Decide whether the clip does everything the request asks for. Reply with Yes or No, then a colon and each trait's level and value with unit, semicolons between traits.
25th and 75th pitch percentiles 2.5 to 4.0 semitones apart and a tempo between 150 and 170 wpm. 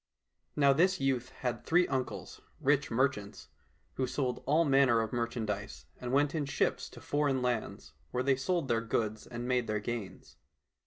Yes: average, 3.1 semitones; average, 165 wpm